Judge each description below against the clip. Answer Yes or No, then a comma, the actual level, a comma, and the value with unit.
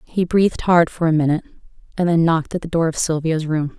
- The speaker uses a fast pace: Yes, fast, 240 wpm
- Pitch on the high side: No, medium, 165 Hz